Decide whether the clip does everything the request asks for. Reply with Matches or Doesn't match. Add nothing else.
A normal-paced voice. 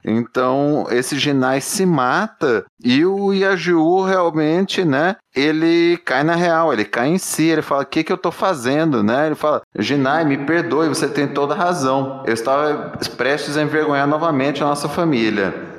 Matches